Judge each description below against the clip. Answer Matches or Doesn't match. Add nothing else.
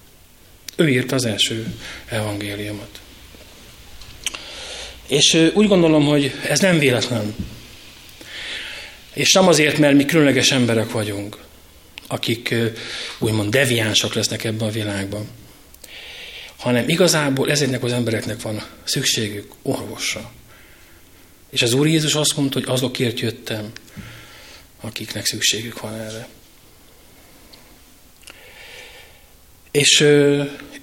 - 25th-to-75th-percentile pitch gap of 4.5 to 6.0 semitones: Matches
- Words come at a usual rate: Doesn't match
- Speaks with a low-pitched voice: Matches